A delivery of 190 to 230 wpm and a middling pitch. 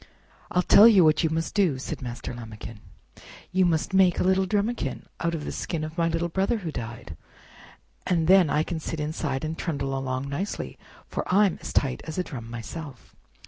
Yes: average, 195 wpm; medium, 160 Hz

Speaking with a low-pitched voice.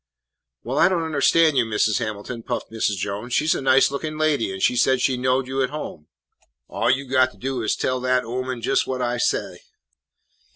Yes: low, 130 Hz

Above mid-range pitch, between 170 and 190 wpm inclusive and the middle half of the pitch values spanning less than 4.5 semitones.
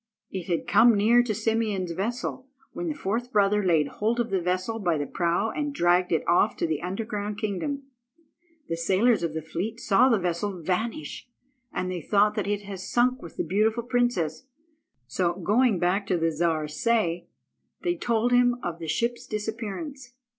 No: high, 205 Hz; average, 180 wpm; average, 5.1 semitones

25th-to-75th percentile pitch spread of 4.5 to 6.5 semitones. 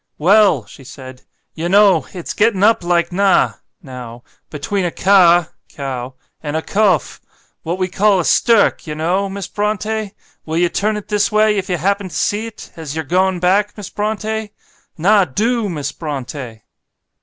Yes: average, 4.9 semitones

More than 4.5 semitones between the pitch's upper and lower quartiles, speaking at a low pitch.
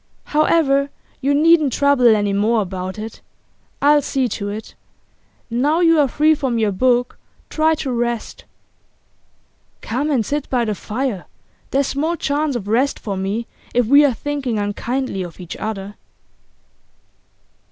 No: average, 5.0 semitones; very high, 250 Hz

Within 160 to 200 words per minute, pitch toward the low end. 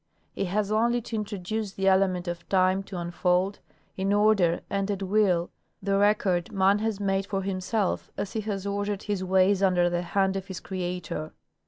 No: average, 180 wpm; high, 195 Hz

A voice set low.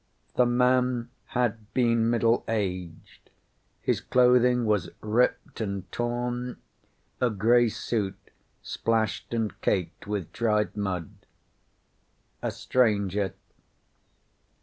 Yes: low, 115 Hz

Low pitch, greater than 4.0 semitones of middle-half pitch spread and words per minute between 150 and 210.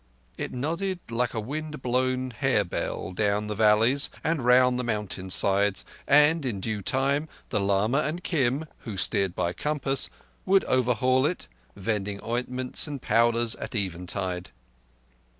No: low, 120 Hz; average, 4.9 semitones; average, 140 wpm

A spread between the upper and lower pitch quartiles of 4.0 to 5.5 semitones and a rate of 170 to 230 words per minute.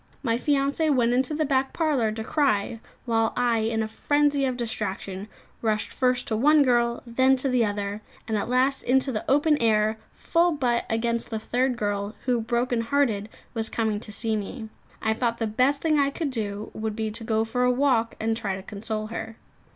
No: average, 3.3 semitones; average, 195 wpm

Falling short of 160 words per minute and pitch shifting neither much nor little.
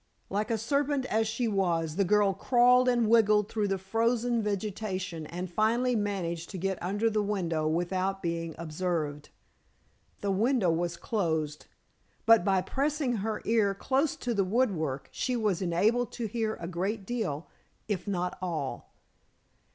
Yes: average, 150 wpm; average, 4.5 semitones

